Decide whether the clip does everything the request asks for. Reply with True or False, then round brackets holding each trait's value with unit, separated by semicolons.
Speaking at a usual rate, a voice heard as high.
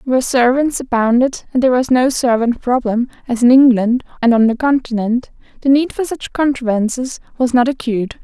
True (175 wpm; 250 Hz)